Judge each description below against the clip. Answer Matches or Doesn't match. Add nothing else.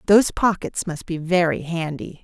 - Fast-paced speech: Doesn't match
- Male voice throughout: Doesn't match